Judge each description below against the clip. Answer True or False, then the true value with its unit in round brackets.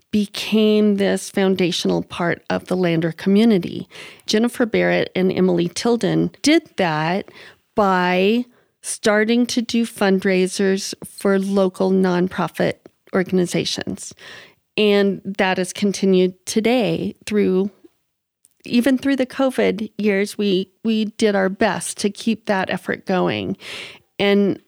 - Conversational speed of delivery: False (110 wpm)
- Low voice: False (200 Hz)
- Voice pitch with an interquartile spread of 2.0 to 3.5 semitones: True (2.9 semitones)